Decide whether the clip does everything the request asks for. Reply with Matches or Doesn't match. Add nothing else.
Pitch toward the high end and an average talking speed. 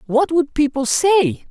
Matches